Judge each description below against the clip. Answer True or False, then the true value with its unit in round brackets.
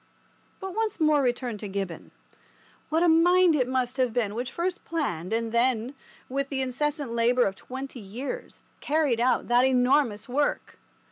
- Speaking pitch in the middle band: False (255 Hz)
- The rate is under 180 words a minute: True (165 wpm)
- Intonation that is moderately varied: True (4.1 semitones)